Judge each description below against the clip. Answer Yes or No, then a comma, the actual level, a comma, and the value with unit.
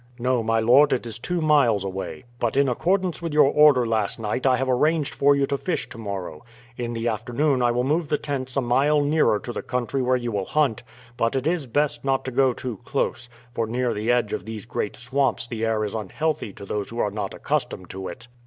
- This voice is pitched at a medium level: No, low, 125 Hz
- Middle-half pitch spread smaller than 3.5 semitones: No, average, 3.9 semitones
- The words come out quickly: Yes, fast, 235 wpm